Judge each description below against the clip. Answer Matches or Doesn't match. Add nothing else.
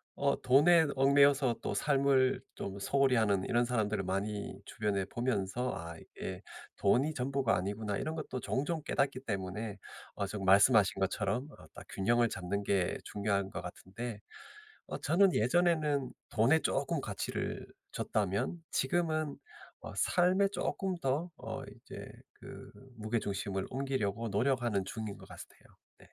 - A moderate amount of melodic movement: Doesn't match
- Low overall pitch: Matches